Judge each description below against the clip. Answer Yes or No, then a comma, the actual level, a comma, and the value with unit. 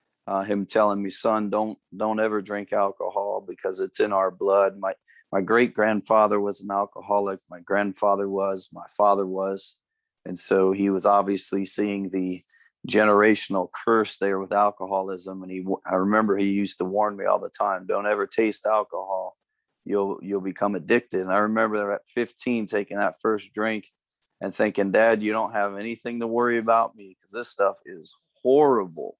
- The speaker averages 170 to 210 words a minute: Yes, average, 175 wpm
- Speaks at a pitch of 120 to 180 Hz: No, low, 100 Hz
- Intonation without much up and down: Yes, narrow, 1.9 semitones